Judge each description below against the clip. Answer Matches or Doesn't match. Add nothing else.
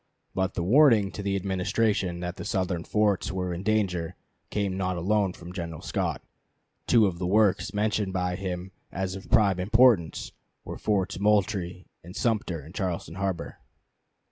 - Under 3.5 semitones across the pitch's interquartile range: Matches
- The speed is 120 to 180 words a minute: Matches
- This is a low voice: Matches